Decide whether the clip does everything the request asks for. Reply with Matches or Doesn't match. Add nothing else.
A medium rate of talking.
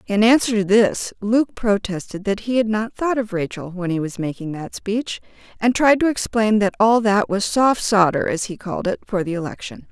Doesn't match